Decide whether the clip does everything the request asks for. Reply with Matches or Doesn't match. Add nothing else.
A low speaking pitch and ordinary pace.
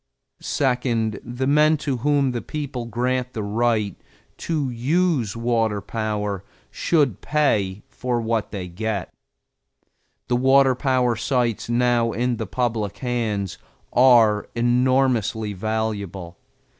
Doesn't match